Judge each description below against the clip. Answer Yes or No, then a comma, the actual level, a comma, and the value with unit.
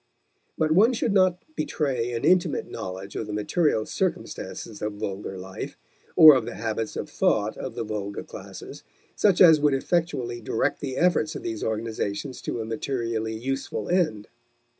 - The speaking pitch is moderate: No, low, 120 Hz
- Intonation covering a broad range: Yes, wide, 6.4 semitones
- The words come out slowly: No, average, 160 wpm